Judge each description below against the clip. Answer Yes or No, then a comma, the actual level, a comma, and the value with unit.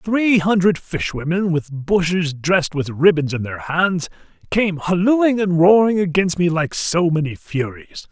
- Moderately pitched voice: Yes, medium, 170 Hz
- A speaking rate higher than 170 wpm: No, average, 155 wpm